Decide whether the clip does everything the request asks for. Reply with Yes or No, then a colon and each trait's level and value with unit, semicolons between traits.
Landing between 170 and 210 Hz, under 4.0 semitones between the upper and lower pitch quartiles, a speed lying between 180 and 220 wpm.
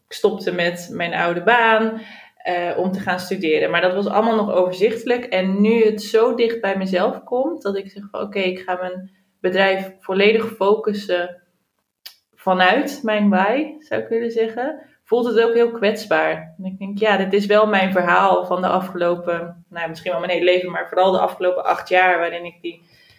Yes: high, 190 Hz; average, 3.5 semitones; average, 195 wpm